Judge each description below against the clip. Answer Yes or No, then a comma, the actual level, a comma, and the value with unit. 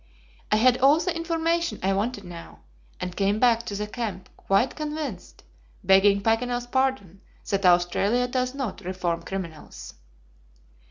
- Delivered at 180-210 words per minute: No, average, 140 wpm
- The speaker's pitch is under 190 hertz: No, high, 215 Hz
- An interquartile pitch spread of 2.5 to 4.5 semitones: No, average, 5.0 semitones